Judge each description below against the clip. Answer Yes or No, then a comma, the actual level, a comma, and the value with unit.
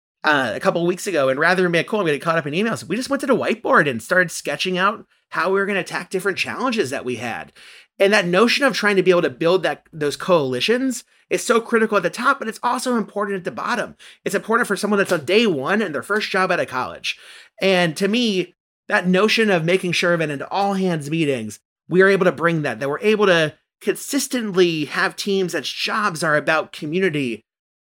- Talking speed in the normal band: No, fast, 240 wpm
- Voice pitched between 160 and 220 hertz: Yes, medium, 185 Hz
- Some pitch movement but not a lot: Yes, average, 4.0 semitones